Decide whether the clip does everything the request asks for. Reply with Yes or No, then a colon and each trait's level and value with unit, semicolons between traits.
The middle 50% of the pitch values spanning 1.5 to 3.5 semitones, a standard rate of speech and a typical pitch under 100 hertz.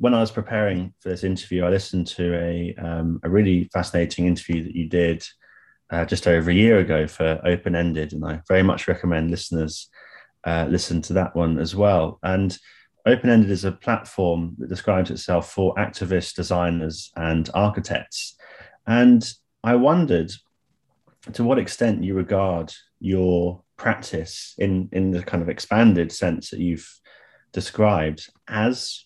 Yes: average, 2.8 semitones; average, 155 wpm; very low, 90 Hz